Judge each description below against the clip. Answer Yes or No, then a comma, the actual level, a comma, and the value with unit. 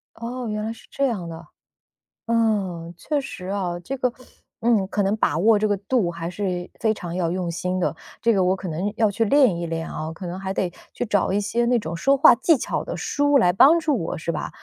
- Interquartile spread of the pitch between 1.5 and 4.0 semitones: No, average, 4.8 semitones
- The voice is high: Yes, high, 200 Hz